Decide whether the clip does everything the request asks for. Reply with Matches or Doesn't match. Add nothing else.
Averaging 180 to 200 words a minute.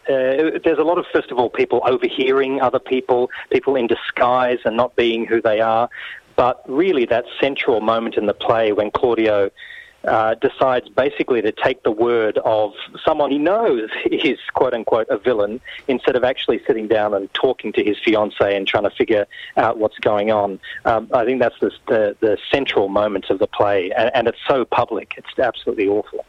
Matches